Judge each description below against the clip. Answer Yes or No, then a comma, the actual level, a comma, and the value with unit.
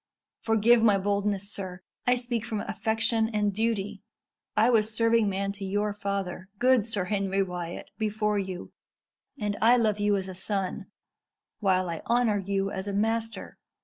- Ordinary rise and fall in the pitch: No, narrow, 2.3 semitones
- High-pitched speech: Yes, high, 205 Hz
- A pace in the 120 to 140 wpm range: No, average, 160 wpm